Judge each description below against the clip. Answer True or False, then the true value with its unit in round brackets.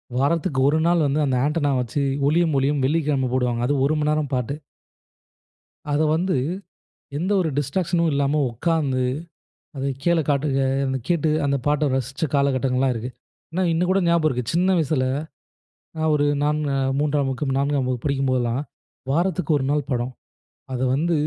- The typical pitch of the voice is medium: True (145 Hz)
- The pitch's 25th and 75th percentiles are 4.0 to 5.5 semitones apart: False (3.3 semitones)